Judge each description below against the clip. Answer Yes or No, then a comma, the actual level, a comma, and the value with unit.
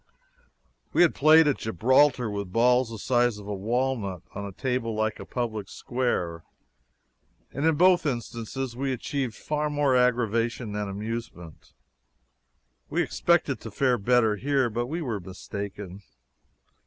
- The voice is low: Yes, low, 120 Hz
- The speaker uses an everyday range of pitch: Yes, average, 4.2 semitones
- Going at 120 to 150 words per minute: Yes, average, 140 wpm